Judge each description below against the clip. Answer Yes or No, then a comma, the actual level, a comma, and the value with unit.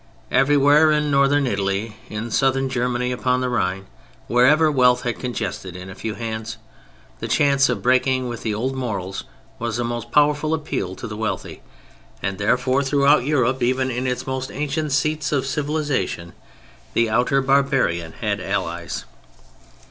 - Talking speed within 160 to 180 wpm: No, average, 150 wpm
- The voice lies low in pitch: Yes, low, 125 Hz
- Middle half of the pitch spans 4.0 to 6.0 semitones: No, average, 3.6 semitones